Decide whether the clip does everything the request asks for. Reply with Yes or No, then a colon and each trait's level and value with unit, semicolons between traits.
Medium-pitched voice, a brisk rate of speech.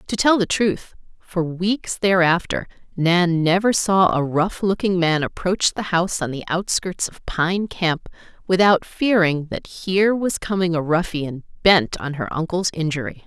No: medium, 175 Hz; average, 165 wpm